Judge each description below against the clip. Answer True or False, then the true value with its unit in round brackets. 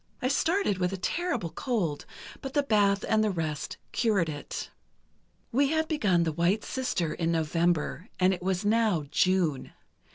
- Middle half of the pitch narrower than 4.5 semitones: False (5.5 semitones)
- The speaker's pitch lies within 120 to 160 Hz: False (190 Hz)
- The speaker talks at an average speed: True (160 wpm)